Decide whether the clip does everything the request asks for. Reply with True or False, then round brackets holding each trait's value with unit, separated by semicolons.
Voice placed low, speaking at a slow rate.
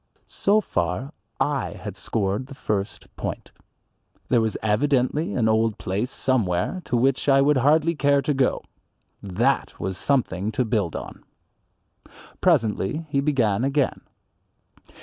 True (125 Hz; 130 wpm)